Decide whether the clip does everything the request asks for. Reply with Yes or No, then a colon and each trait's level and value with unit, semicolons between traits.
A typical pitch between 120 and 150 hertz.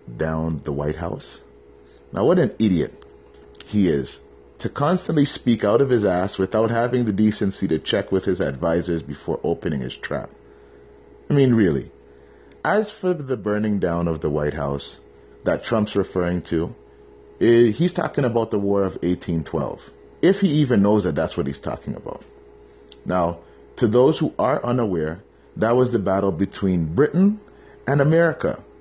No: very low, 95 Hz